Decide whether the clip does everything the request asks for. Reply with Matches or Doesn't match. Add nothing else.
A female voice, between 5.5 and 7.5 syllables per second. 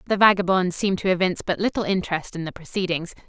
Matches